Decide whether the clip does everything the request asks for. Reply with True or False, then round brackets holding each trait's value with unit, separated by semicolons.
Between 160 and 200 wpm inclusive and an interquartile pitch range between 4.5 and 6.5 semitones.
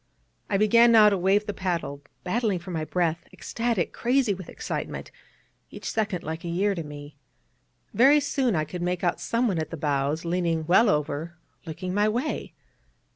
True (175 wpm; 4.8 semitones)